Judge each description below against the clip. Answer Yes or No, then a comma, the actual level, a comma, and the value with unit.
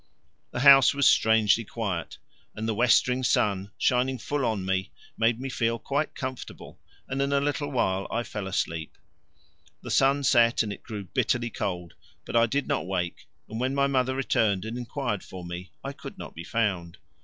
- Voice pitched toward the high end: No, low, 115 Hz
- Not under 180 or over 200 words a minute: Yes, average, 185 wpm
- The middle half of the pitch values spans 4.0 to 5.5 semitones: Yes, average, 5.1 semitones